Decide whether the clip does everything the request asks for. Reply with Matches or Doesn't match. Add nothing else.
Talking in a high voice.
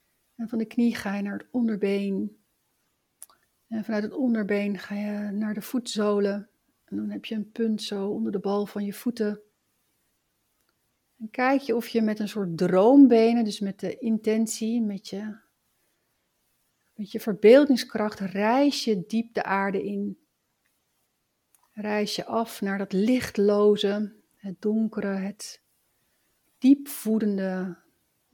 Matches